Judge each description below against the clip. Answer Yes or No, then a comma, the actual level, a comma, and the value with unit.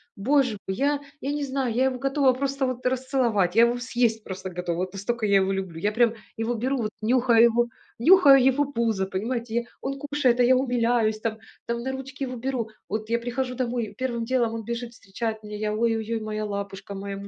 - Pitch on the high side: Yes, high, 235 Hz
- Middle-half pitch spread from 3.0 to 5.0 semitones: Yes, average, 3.3 semitones